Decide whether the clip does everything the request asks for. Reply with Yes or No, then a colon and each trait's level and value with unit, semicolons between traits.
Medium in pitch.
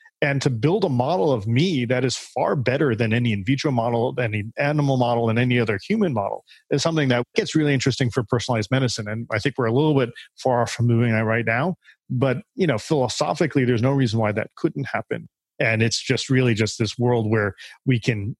No: low, 125 Hz